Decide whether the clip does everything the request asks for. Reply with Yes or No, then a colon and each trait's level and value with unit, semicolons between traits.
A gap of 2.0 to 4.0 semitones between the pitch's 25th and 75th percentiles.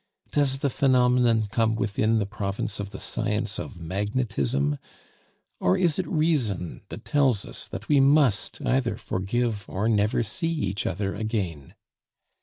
No: average, 4.6 semitones